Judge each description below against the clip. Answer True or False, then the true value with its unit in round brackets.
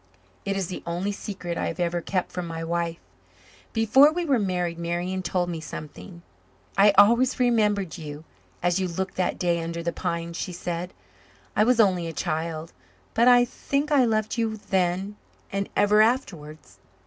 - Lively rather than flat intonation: False (4.0 semitones)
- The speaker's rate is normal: True (170 wpm)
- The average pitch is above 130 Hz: True (185 Hz)